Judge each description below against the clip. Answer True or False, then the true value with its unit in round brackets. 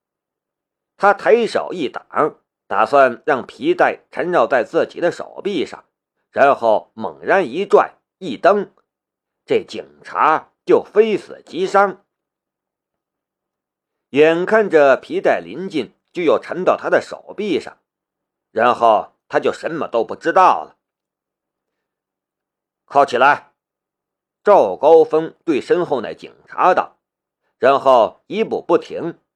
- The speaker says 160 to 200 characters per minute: True (165 characters per minute)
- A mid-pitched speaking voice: False (360 Hz)